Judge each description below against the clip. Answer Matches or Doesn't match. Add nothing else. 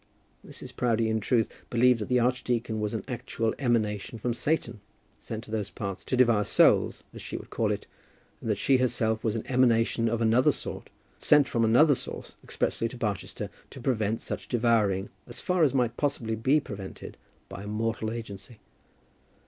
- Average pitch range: Doesn't match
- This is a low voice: Matches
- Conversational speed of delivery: Matches